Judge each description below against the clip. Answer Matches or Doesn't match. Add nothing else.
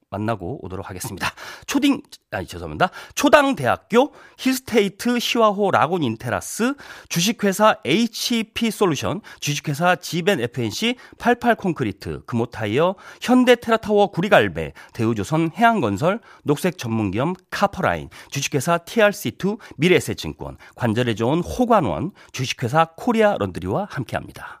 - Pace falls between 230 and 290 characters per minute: Doesn't match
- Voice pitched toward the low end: Doesn't match